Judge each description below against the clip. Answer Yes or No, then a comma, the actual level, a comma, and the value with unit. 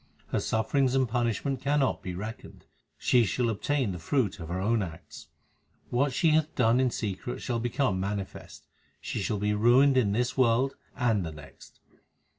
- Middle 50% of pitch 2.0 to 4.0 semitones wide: No, average, 4.5 semitones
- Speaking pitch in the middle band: No, low, 115 Hz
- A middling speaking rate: Yes, average, 170 wpm